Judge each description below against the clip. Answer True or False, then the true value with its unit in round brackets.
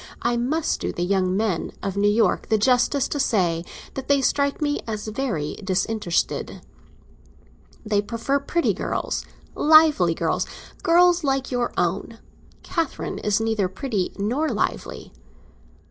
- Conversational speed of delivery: False (130 wpm)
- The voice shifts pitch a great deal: True (5.9 semitones)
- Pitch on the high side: True (230 Hz)